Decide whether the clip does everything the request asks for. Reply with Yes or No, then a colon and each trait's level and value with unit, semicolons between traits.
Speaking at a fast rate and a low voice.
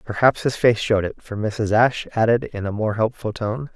Yes: fast, 225 wpm; low, 110 Hz